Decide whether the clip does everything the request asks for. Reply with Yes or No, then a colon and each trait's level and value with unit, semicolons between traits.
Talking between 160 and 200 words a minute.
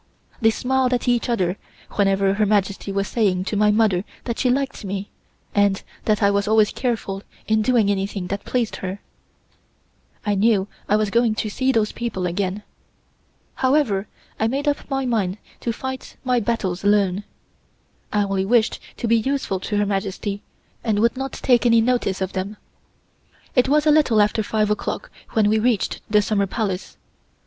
Yes: average, 175 wpm